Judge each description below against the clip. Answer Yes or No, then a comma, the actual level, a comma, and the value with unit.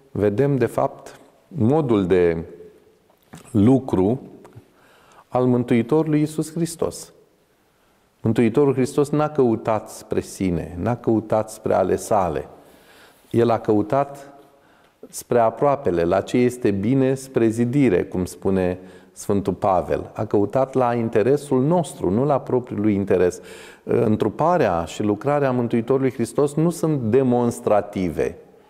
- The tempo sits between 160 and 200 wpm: No, slow, 115 wpm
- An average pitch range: Yes, average, 4.2 semitones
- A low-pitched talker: Yes, low, 125 Hz